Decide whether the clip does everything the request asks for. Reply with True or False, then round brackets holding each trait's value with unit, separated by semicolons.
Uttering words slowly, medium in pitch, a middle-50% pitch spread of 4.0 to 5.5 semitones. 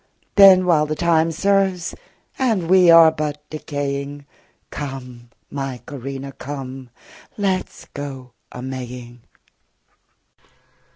True (100 wpm; 145 Hz; 4.3 semitones)